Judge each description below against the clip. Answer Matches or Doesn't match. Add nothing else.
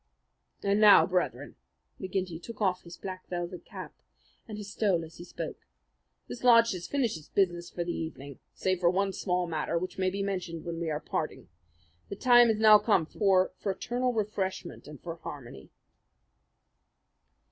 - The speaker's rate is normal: Matches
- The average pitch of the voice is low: Doesn't match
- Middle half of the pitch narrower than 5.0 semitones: Matches